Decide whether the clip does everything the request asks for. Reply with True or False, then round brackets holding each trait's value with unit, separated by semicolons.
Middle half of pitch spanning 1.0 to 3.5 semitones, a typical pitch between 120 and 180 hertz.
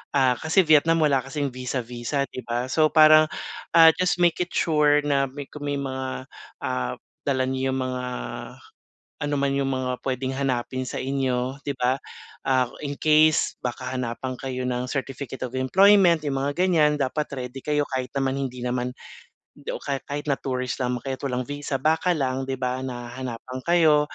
True (2.5 semitones; 135 Hz)